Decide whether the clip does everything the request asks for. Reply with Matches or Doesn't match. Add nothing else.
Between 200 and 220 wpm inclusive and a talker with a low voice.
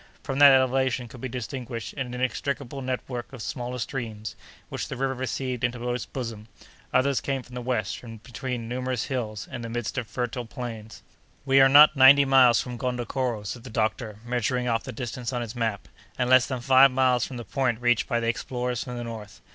Matches